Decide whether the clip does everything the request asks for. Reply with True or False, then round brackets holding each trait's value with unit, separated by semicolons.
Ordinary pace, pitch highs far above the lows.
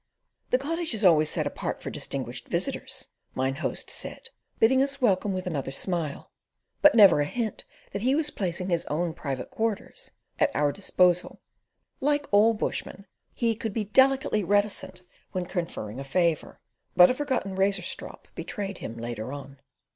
True (160 wpm; 5.9 semitones)